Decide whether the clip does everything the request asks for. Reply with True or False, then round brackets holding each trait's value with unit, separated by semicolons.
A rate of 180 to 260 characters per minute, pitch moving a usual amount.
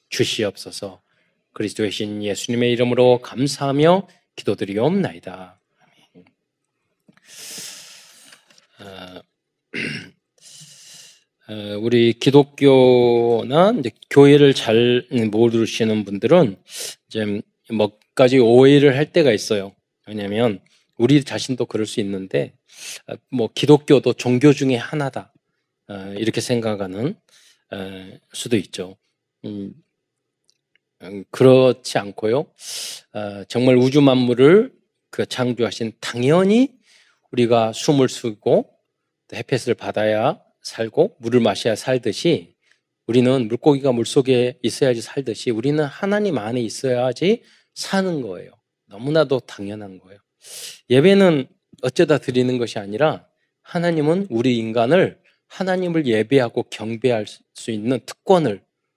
True (230 characters per minute; 4.9 semitones)